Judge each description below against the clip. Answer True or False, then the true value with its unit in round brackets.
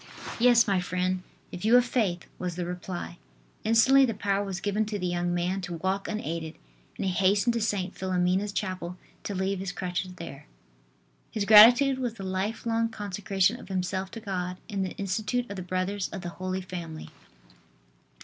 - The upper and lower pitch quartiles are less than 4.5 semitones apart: True (2.7 semitones)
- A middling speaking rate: True (180 wpm)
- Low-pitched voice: False (190 Hz)